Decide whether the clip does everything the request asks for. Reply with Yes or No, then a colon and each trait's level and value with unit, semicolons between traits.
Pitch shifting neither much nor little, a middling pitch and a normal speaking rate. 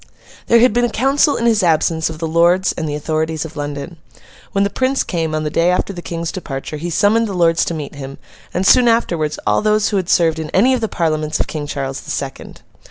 No: average, 4.9 semitones; medium, 170 Hz; fast, 240 wpm